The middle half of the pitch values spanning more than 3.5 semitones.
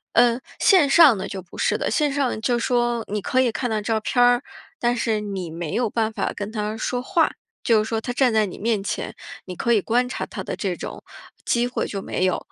No: average, 2.7 semitones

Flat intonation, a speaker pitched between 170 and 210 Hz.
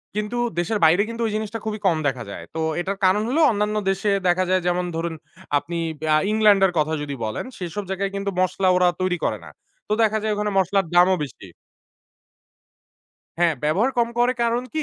No: average, 3.4 semitones; high, 190 Hz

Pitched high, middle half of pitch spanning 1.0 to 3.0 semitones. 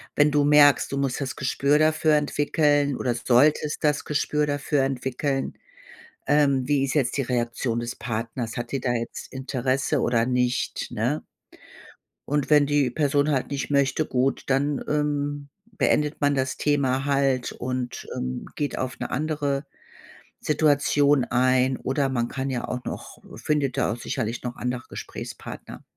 No: low, 135 Hz; narrow, 2.5 semitones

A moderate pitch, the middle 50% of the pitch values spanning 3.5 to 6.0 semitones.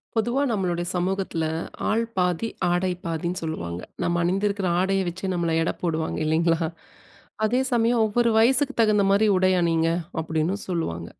Yes: medium, 180 Hz; average, 4.1 semitones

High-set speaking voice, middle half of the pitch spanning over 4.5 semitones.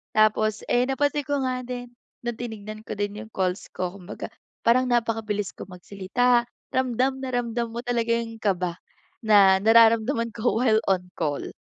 No: high, 230 Hz; average, 2.9 semitones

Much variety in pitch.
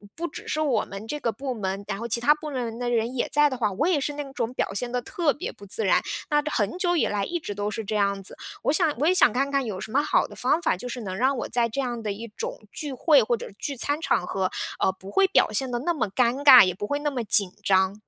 Yes: wide, 5.8 semitones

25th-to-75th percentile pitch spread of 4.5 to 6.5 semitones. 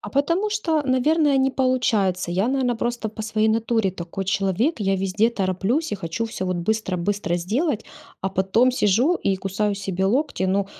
Yes: average, 5.2 semitones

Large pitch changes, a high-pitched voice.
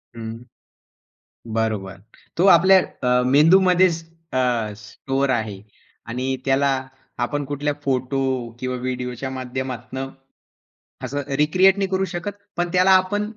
No: wide, 5.9 semitones; low, 135 Hz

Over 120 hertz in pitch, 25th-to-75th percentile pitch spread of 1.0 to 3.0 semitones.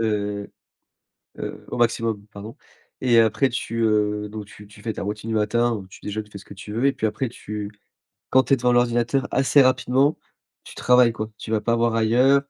No: low, 115 Hz; narrow, 2.6 semitones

